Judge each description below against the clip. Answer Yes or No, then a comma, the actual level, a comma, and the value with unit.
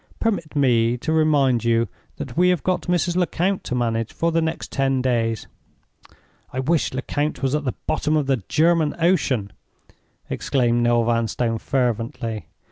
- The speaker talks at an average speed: Yes, average, 155 wpm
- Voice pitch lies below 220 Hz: Yes, low, 135 Hz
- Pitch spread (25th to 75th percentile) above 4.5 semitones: Yes, average, 5.3 semitones